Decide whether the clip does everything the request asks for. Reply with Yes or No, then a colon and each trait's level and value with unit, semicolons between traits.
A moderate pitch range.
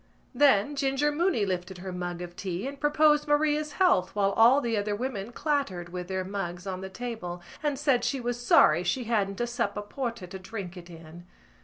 No: wide, 6.9 semitones